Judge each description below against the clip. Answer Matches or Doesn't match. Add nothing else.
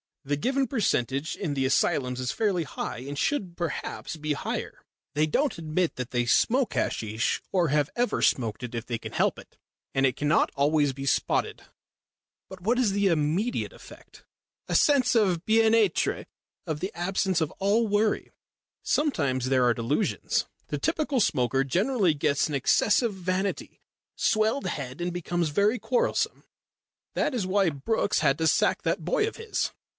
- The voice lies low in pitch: Doesn't match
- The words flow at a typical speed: Matches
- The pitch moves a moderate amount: Doesn't match